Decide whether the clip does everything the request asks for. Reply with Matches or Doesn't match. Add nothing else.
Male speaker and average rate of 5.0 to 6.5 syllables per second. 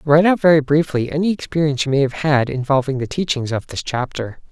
Matches